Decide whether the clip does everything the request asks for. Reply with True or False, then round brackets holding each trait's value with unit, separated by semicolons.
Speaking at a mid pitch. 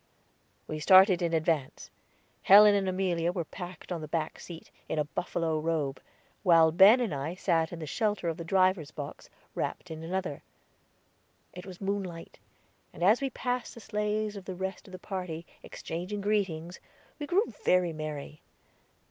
True (180 Hz)